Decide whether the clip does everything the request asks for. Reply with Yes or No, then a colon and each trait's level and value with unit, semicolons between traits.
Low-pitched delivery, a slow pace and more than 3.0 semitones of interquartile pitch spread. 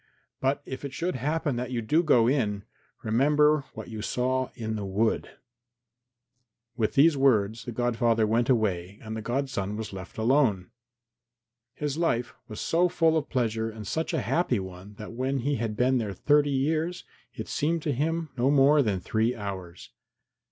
No: low, 125 Hz; average, 175 wpm; average, 4.8 semitones